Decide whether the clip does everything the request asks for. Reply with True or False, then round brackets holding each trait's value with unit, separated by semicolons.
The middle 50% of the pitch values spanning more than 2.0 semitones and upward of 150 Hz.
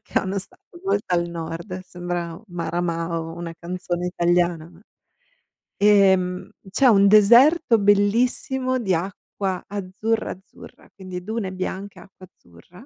True (2.9 semitones; 185 Hz)